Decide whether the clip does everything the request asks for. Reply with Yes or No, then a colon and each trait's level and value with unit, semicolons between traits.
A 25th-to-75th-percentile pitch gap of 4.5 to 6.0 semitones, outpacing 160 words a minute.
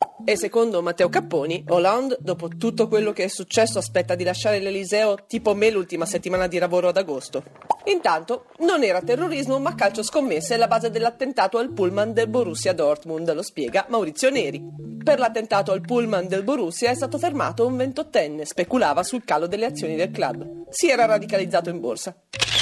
Yes: average, 5.2 semitones; fast, 170 wpm